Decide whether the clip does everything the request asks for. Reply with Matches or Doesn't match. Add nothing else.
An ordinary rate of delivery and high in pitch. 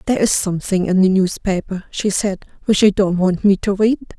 Doesn't match